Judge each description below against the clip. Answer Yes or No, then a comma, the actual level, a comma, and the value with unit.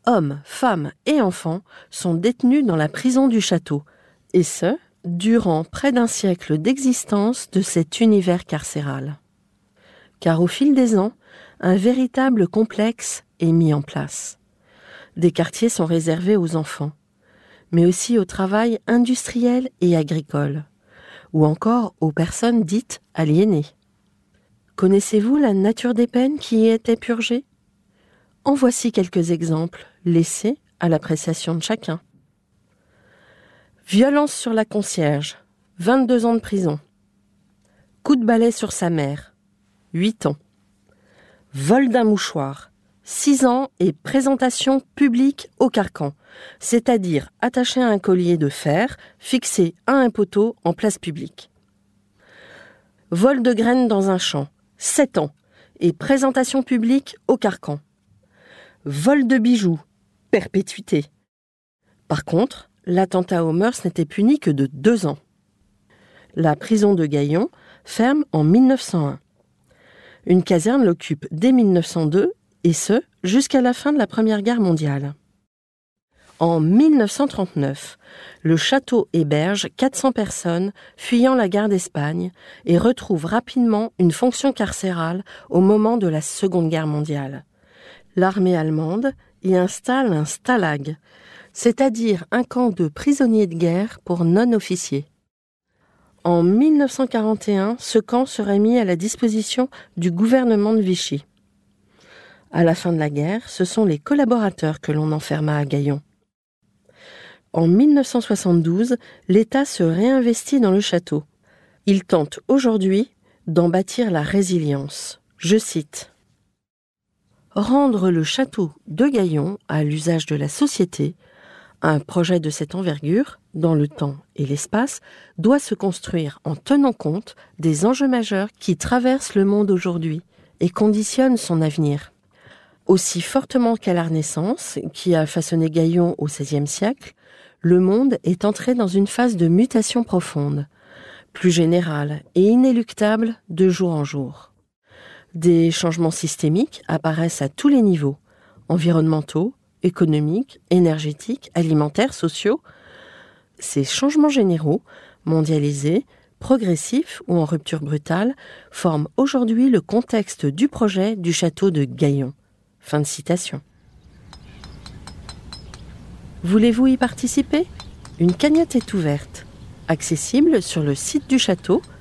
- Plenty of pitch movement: Yes, wide, 6.7 semitones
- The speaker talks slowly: Yes, slow, 125 wpm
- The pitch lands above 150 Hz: Yes, medium, 185 Hz